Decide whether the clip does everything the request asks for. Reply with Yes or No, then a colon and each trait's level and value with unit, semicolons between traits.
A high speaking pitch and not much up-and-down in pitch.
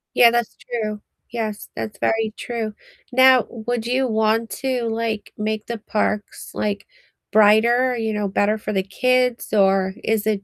Yes: high, 220 Hz; narrow, 2.2 semitones